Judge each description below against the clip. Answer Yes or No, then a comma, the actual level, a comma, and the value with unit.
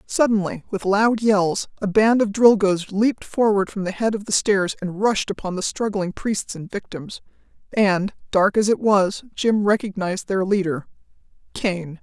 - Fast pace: No, average, 165 wpm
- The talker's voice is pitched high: Yes, high, 200 Hz